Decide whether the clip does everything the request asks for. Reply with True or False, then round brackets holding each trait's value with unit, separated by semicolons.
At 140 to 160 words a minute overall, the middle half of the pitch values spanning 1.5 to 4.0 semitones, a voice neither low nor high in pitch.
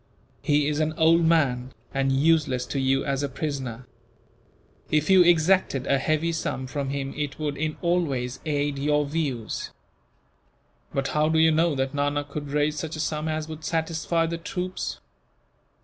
False (170 wpm; 2.7 semitones; 150 Hz)